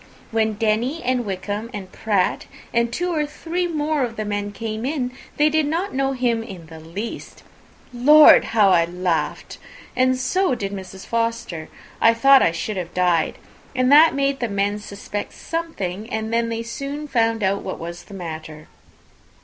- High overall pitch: Yes, high, 225 Hz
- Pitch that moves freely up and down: Yes, wide, 5.7 semitones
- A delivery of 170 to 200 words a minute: Yes, average, 175 wpm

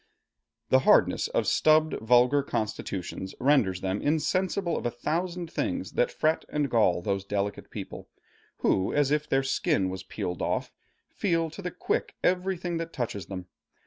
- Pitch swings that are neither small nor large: No, wide, 8.7 semitones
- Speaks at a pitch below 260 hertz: Yes, medium, 140 Hz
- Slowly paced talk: No, average, 155 wpm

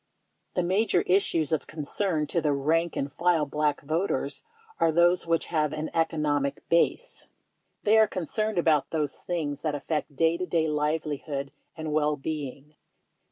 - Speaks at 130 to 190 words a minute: Yes, average, 160 wpm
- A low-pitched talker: No, medium, 155 Hz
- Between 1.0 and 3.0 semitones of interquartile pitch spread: Yes, narrow, 2.5 semitones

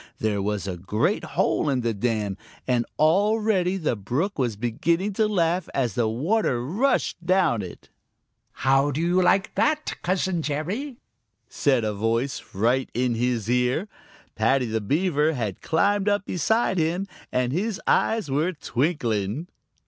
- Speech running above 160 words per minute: No, average, 150 wpm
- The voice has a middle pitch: Yes, medium, 145 Hz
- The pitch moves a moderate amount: No, wide, 8.0 semitones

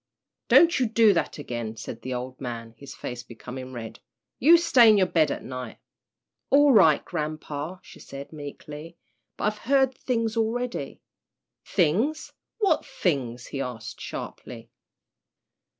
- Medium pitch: Yes, medium, 155 Hz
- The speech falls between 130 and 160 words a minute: Yes, average, 140 wpm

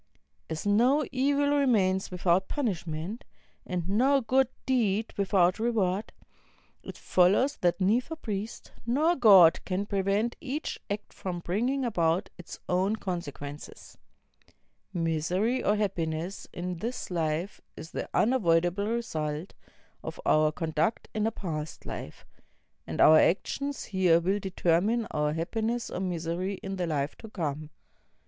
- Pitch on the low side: No, high, 190 Hz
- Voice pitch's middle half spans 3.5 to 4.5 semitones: No, average, 5.2 semitones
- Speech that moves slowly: Yes, slow, 130 wpm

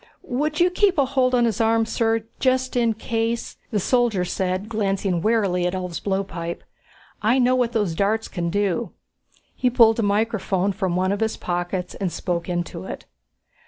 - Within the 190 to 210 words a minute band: No, average, 175 wpm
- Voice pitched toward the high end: Yes, high, 215 Hz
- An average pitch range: Yes, average, 4.3 semitones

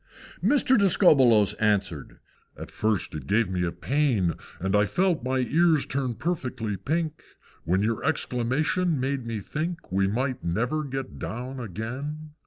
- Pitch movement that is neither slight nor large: No, wide, 6.6 semitones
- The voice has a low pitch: Yes, low, 125 Hz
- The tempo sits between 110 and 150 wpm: Yes, average, 145 wpm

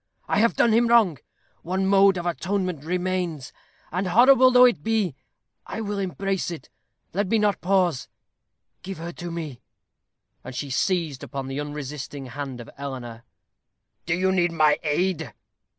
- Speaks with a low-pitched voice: No, medium, 175 Hz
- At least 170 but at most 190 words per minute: No, average, 155 wpm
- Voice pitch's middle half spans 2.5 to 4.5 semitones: No, average, 4.9 semitones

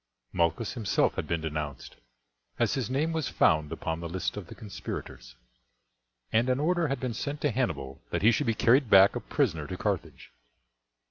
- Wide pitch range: Yes, wide, 8.1 semitones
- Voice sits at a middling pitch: No, low, 105 Hz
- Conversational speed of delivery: Yes, average, 185 wpm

